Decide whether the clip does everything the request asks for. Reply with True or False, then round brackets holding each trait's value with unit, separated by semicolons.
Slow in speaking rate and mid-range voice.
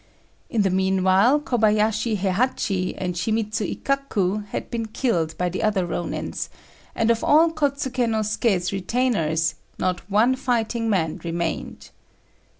False (130 wpm; 210 Hz)